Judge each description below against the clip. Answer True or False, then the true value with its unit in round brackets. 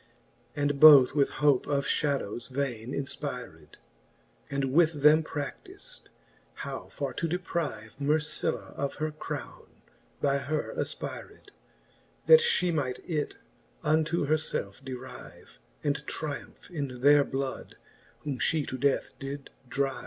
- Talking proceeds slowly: True (125 wpm)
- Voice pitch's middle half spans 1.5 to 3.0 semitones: True (2.4 semitones)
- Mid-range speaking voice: True (145 Hz)